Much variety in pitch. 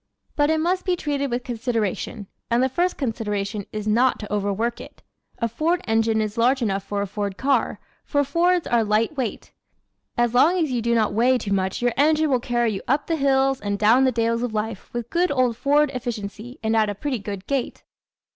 No: average, 4.4 semitones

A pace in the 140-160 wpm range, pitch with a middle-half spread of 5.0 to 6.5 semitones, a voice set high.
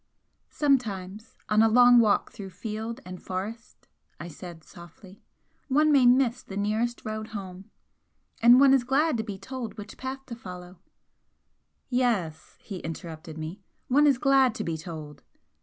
Yes: average, 155 wpm; average, 5.3 semitones; high, 215 Hz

